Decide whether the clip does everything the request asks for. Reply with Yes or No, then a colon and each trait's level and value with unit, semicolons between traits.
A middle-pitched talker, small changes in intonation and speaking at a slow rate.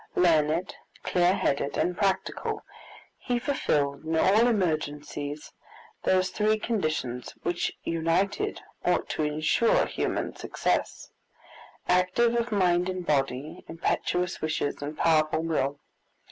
No: medium, 165 Hz; average, 3.8 semitones; slow, 110 wpm